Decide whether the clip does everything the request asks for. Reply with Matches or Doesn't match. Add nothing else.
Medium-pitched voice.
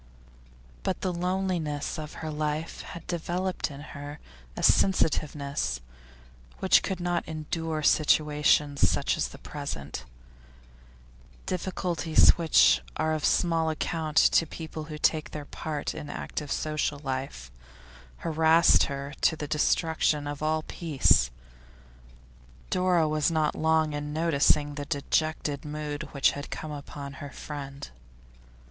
Matches